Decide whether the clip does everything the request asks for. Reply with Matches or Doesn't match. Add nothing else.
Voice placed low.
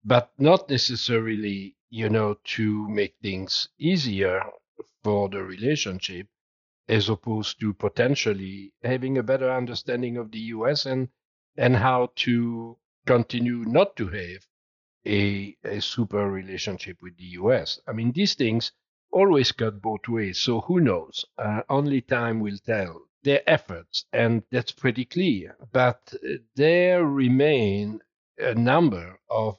Matches